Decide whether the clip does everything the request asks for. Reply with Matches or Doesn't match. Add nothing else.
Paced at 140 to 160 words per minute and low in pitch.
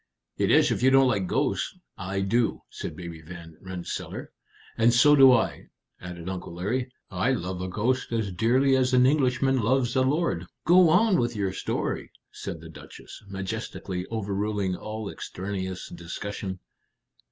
Matches